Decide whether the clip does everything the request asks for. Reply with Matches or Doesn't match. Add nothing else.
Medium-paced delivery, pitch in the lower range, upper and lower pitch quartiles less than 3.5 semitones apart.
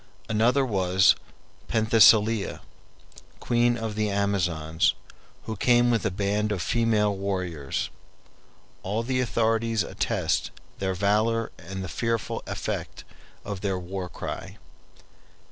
Doesn't match